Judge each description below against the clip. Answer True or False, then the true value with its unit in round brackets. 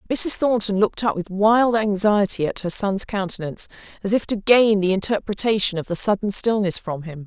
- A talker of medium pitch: False (200 Hz)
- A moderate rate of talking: True (180 wpm)